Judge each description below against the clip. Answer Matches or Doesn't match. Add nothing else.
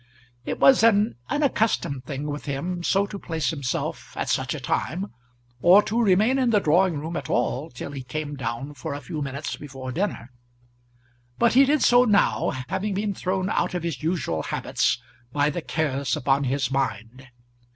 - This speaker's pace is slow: Doesn't match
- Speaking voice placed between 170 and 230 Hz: Doesn't match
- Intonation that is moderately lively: Doesn't match